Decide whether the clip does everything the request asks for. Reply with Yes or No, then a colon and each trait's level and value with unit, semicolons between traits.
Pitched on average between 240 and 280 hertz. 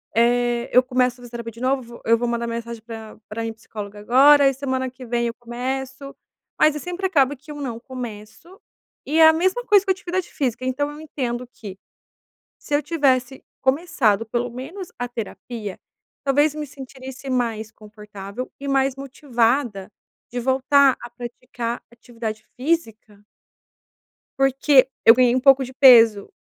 Yes: very high, 250 Hz